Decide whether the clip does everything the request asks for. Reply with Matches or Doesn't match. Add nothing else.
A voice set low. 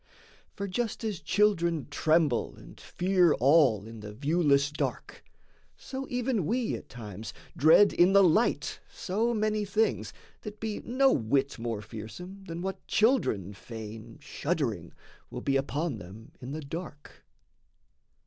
Doesn't match